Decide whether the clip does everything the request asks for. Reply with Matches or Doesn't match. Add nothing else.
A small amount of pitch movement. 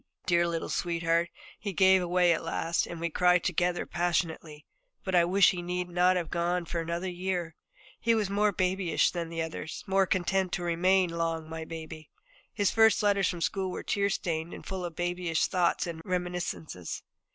Matches